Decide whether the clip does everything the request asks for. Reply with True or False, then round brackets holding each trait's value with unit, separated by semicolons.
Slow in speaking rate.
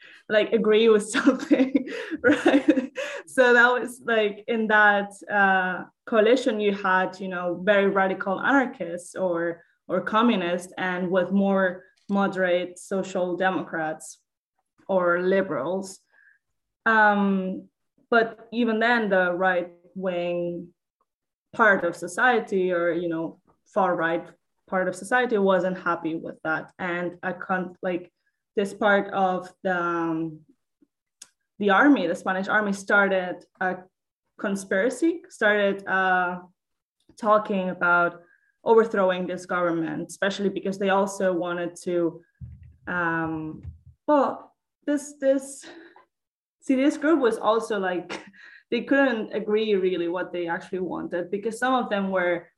True (120 wpm)